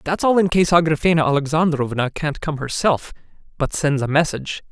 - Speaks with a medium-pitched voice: Yes, medium, 155 Hz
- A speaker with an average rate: Yes, average, 165 wpm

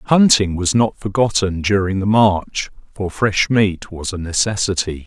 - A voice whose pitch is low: Yes, low, 100 Hz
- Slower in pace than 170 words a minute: Yes, average, 155 wpm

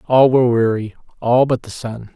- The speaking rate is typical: Yes, average, 195 wpm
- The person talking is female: No, male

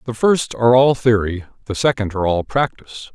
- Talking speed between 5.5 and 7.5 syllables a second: Yes, 5.8 syllables/s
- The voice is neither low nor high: No, low, 115 Hz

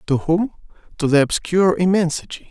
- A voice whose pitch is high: No, medium, 170 Hz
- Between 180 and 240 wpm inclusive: No, average, 145 wpm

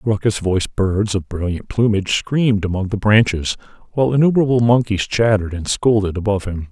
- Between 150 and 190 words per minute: Yes, average, 160 wpm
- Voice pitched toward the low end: Yes, low, 105 Hz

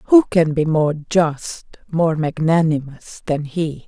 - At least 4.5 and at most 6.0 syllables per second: No, 3.4 syllables/s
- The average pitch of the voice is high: No, medium, 160 Hz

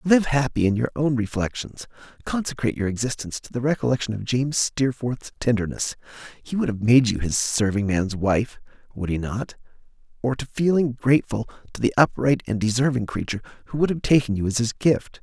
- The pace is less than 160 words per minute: No, average, 175 wpm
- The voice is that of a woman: No, male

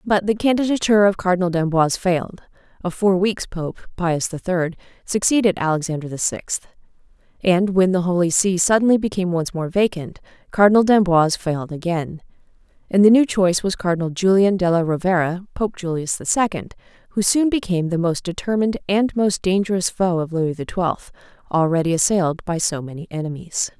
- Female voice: Yes, female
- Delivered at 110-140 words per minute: No, average, 165 wpm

